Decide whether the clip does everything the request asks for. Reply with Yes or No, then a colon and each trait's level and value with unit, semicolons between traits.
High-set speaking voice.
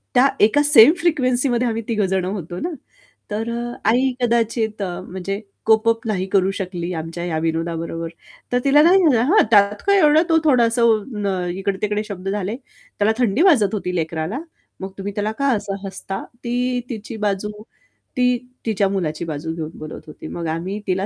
Yes: high, 205 Hz